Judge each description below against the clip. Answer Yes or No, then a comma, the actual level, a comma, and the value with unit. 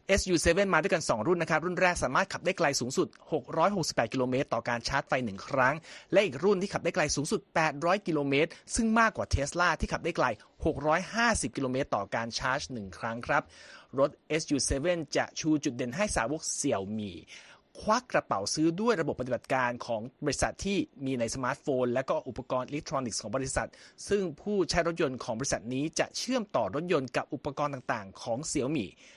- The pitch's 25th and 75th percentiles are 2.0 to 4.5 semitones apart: No, wide, 5.4 semitones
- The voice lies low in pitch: No, medium, 155 Hz